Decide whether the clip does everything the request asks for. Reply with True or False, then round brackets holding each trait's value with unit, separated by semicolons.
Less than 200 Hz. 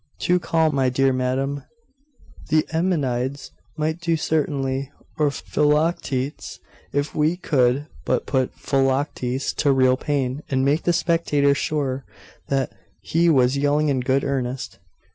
True (140 Hz)